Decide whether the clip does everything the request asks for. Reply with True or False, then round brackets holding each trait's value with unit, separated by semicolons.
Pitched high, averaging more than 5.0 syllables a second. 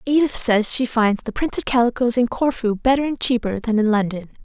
True (235 Hz; 5.5 syllables/s)